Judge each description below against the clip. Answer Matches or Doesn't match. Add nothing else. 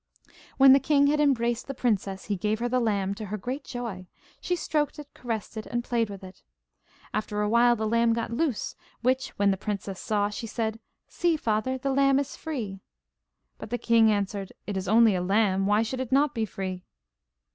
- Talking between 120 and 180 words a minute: Doesn't match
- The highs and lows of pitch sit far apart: Doesn't match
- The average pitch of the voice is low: Doesn't match